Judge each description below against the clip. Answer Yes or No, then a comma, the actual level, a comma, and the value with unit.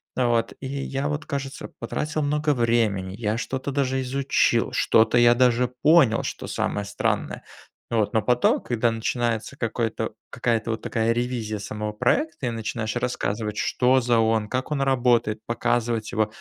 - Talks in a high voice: No, low, 120 Hz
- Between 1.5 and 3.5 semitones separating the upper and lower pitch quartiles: Yes, average, 2.9 semitones